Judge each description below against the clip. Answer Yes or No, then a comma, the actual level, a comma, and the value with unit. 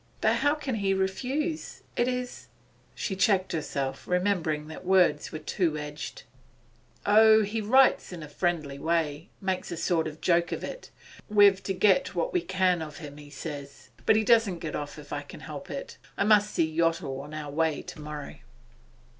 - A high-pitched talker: No, medium, 180 Hz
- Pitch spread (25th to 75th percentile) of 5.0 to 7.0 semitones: Yes, wide, 5.6 semitones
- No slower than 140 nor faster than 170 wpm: No, average, 190 wpm